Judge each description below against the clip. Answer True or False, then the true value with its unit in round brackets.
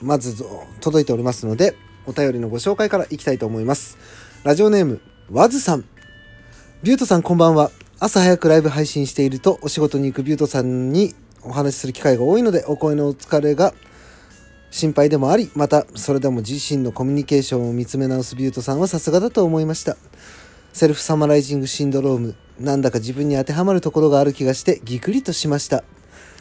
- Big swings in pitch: False (3.8 semitones)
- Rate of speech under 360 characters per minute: False (450 characters per minute)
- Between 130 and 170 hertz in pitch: True (140 Hz)